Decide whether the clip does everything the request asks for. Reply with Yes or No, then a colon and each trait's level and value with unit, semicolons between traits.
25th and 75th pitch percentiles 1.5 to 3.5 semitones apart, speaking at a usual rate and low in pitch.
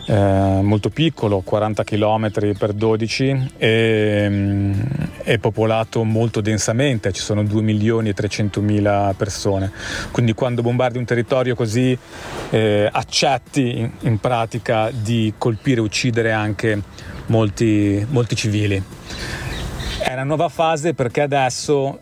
Yes: average, 2.9 semitones; average, 125 wpm; low, 110 Hz